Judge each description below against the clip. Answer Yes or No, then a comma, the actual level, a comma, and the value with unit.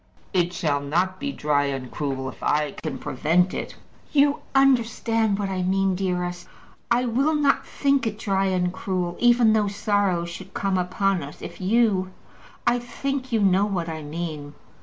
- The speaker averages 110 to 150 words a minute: No, average, 170 wpm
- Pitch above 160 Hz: Yes, high, 190 Hz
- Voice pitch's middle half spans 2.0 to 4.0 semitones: No, average, 4.9 semitones